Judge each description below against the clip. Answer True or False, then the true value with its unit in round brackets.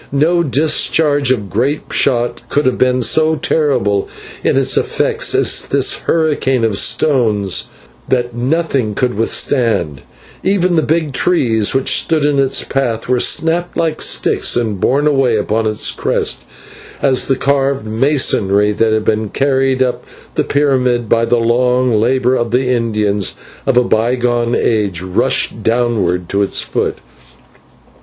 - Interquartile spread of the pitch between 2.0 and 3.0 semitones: False (4.0 semitones)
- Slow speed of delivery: False (150 wpm)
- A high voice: False (125 Hz)